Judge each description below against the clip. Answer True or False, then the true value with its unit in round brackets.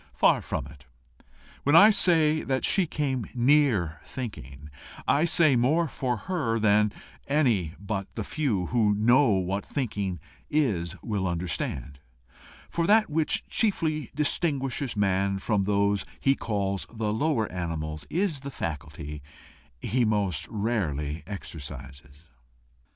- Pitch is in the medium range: False (105 Hz)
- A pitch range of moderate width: False (7.8 semitones)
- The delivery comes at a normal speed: False (125 wpm)